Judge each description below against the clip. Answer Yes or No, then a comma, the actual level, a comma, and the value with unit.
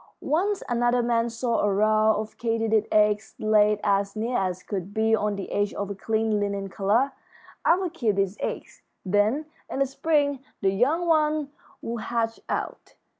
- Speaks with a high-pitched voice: Yes, high, 220 Hz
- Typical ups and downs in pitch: Yes, average, 3.2 semitones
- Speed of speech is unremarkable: Yes, average, 170 wpm